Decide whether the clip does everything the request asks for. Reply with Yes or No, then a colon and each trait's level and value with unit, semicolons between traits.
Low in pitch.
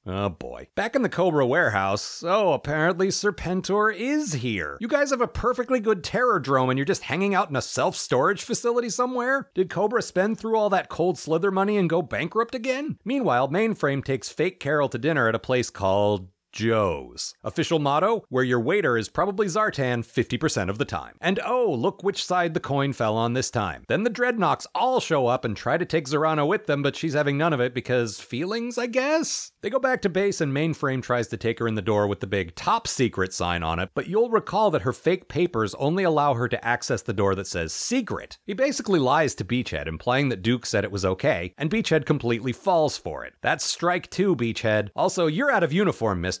No: medium, 155 Hz